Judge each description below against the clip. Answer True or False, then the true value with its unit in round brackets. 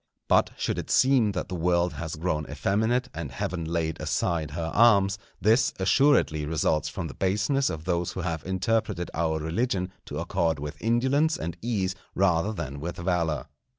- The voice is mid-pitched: False (90 Hz)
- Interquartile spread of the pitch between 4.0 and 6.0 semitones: True (4.6 semitones)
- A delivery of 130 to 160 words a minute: False (170 wpm)